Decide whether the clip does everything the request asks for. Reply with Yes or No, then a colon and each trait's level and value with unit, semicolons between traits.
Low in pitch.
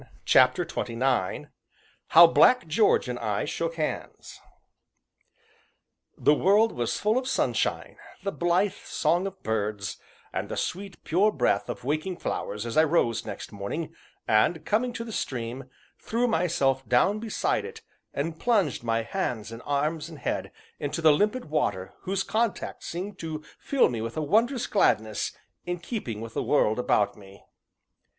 No: medium, 155 Hz